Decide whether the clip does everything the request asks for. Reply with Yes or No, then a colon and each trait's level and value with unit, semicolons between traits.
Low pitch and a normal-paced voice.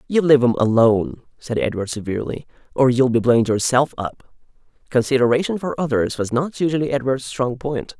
Yes: low, 130 Hz; average, 165 wpm